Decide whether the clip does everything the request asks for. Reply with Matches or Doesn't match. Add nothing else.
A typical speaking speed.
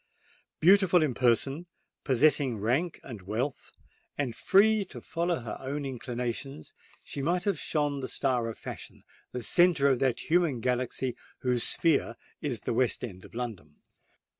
Matches